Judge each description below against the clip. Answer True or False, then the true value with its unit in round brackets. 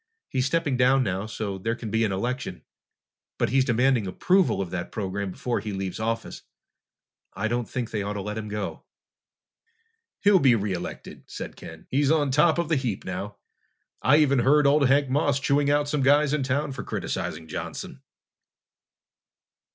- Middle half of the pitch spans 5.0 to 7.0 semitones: True (5.6 semitones)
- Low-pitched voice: True (125 Hz)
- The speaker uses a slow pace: False (175 wpm)